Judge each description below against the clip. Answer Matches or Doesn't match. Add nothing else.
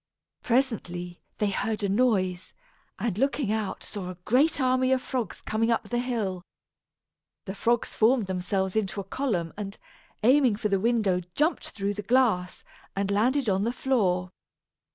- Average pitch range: Matches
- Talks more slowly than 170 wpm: Matches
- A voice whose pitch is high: Matches